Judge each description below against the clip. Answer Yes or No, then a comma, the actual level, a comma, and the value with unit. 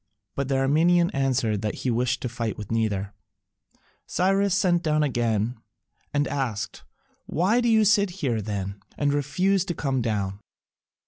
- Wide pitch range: Yes, wide, 7.6 semitones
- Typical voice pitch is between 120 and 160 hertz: Yes, low, 135 Hz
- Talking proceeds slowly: No, average, 145 wpm